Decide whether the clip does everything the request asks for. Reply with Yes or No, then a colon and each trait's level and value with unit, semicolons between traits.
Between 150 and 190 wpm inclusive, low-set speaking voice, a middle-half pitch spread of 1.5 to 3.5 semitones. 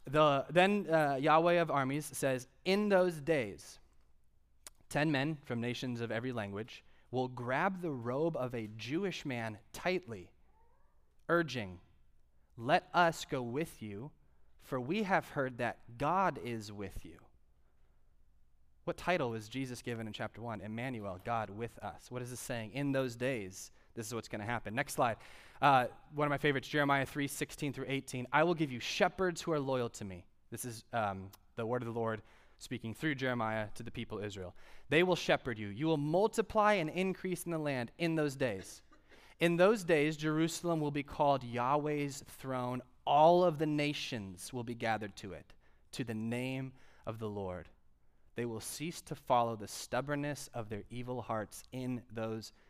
No: average, 180 wpm; low, 125 Hz; wide, 5.5 semitones